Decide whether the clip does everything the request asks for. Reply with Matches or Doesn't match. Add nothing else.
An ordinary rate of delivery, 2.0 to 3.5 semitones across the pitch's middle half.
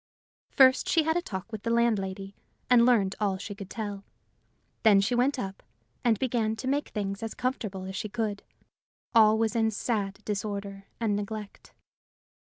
Matches